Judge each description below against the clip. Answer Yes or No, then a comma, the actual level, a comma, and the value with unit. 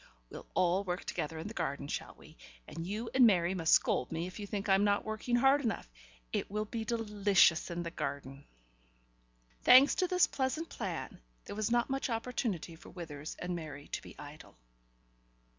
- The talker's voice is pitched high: Yes, high, 195 Hz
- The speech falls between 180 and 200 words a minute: Yes, average, 185 wpm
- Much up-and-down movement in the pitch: Yes, wide, 5.7 semitones